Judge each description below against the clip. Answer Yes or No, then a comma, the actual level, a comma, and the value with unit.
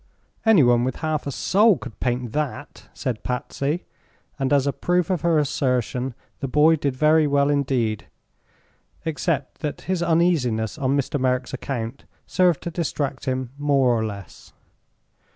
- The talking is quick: No, average, 150 wpm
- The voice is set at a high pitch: No, medium, 140 Hz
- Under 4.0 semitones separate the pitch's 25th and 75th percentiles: Yes, average, 3.6 semitones